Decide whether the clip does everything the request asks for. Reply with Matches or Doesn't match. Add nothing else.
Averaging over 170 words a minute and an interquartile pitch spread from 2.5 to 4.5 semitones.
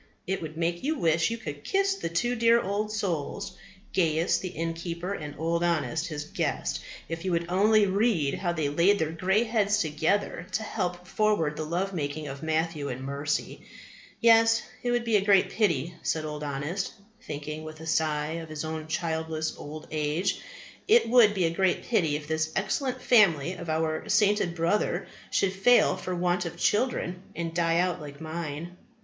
Matches